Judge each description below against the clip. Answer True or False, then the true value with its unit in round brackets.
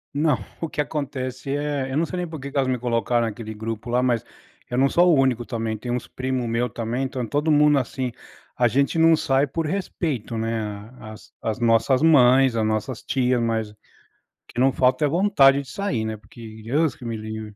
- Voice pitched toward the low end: True (125 Hz)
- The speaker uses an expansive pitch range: False (3.6 semitones)